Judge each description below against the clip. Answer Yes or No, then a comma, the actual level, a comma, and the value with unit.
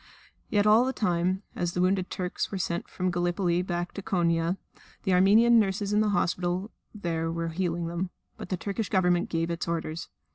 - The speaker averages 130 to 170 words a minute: No, average, 195 wpm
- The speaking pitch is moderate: Yes, medium, 180 Hz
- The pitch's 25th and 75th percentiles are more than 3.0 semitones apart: No, narrow, 2.4 semitones